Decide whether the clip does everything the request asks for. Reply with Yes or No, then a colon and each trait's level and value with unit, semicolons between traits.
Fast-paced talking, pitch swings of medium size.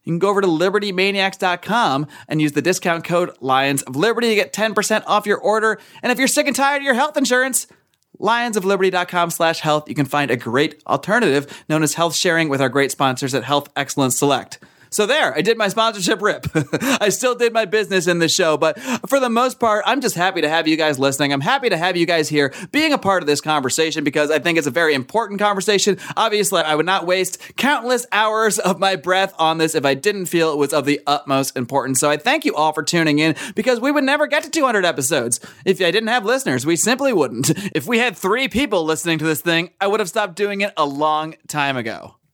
No: fast, 235 wpm; wide, 6.0 semitones